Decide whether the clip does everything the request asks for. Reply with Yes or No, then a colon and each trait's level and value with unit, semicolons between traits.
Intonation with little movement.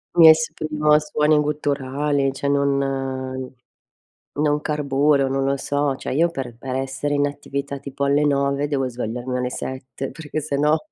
Yes: narrow, 1.8 semitones